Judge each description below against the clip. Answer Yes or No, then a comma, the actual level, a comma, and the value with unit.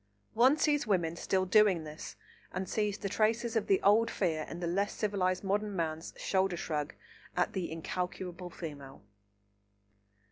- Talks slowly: No, average, 150 wpm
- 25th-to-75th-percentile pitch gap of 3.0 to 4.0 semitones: Yes, average, 3.7 semitones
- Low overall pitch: No, medium, 185 Hz